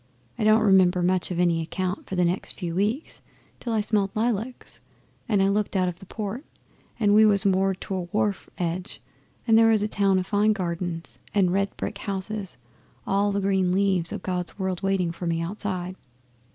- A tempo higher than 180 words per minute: Yes, average, 200 wpm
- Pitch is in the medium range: No, high, 195 Hz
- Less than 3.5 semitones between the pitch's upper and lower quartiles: Yes, narrow, 2.4 semitones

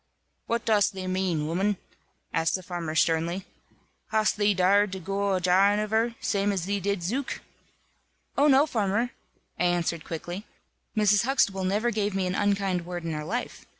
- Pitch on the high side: Yes, high, 195 Hz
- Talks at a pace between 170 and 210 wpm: Yes, average, 175 wpm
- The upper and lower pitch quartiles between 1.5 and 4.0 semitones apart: Yes, average, 2.8 semitones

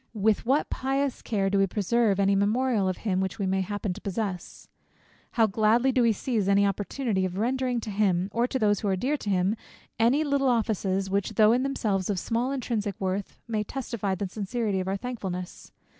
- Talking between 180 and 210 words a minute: Yes, fast, 205 wpm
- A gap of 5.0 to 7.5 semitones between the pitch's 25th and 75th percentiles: No, average, 3.7 semitones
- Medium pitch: No, high, 210 Hz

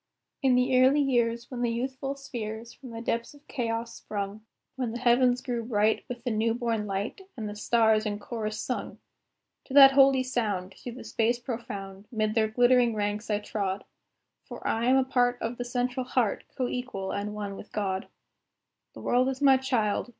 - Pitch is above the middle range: Yes, high, 235 Hz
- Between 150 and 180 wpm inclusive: No, average, 190 wpm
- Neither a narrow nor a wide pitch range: Yes, average, 3.0 semitones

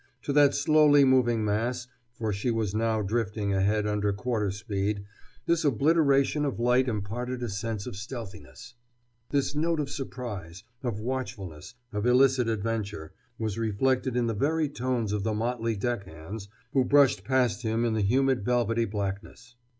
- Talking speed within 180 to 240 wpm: No, average, 155 wpm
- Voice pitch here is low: Yes, low, 115 Hz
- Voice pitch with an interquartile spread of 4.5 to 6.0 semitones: No, average, 4.0 semitones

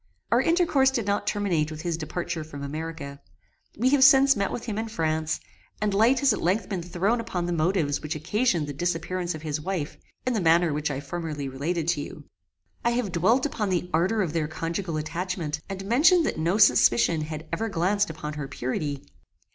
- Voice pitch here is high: No, medium, 175 Hz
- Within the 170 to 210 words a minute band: Yes, average, 200 wpm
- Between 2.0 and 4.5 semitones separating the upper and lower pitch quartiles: No, average, 5.2 semitones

